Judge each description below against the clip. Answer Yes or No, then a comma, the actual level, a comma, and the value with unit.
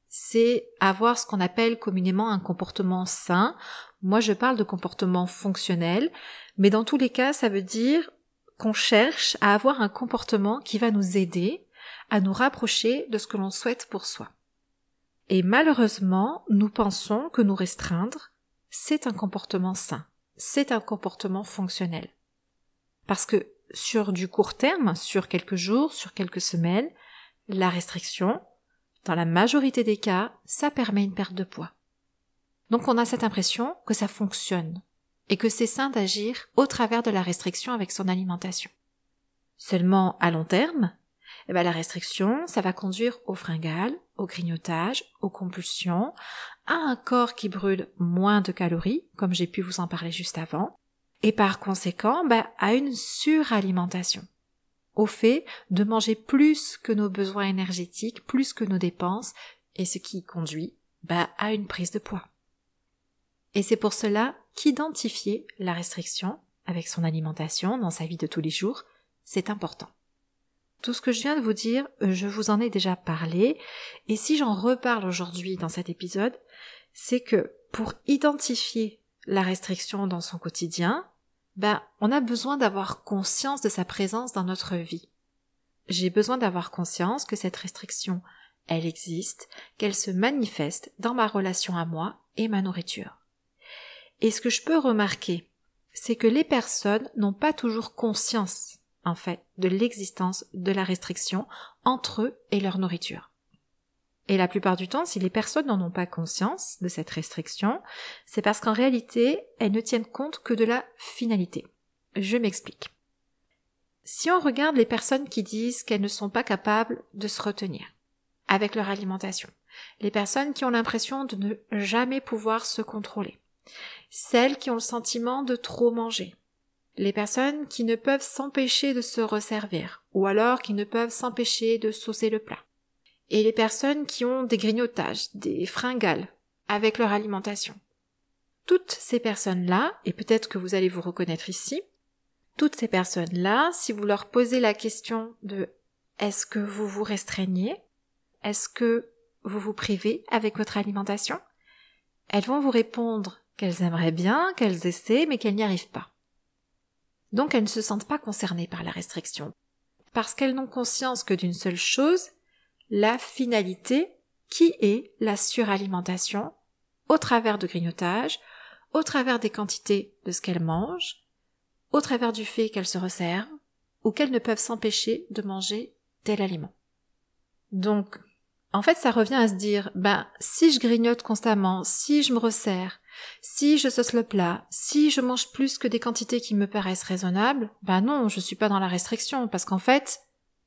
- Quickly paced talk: No, average, 165 wpm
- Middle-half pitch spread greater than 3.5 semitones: Yes, average, 4.3 semitones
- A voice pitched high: Yes, high, 210 Hz